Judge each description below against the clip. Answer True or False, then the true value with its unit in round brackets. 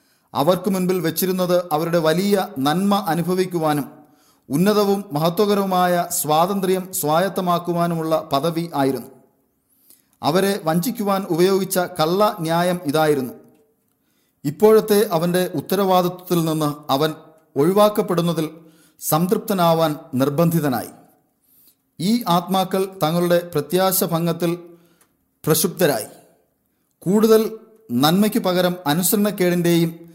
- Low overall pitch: False (175 Hz)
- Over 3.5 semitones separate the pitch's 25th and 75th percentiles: False (3.2 semitones)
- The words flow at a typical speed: False (75 wpm)